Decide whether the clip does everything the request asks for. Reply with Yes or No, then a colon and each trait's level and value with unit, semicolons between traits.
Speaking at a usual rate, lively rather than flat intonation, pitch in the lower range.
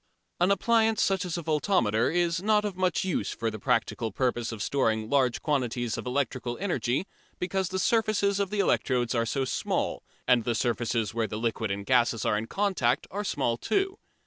Yes: average, 185 wpm; wide, 8.6 semitones; low, 130 Hz